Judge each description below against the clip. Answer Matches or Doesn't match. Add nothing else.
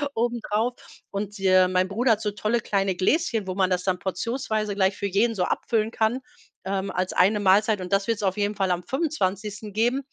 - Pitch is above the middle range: Matches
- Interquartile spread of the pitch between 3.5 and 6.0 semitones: Doesn't match